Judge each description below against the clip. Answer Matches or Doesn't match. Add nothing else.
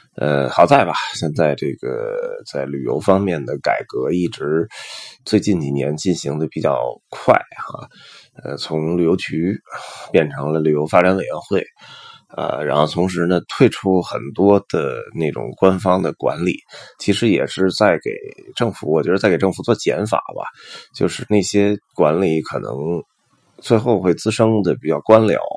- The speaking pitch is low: Matches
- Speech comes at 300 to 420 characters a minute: Doesn't match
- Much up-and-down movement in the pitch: Doesn't match